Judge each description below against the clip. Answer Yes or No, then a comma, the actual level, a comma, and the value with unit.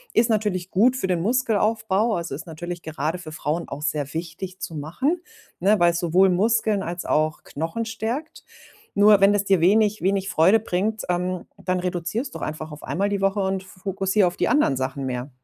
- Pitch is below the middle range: No, medium, 185 Hz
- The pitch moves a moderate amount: Yes, average, 4.1 semitones